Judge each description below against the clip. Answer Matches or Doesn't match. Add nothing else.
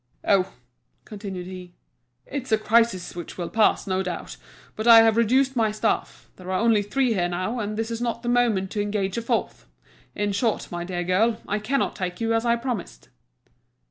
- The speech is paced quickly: Doesn't match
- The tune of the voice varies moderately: Matches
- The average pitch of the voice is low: Doesn't match